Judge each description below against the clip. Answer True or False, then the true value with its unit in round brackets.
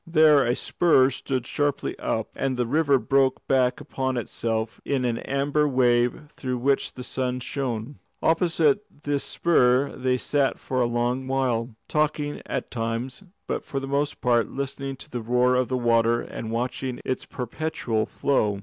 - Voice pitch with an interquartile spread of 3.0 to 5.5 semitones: False (2.5 semitones)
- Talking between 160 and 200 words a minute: True (165 wpm)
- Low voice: True (130 Hz)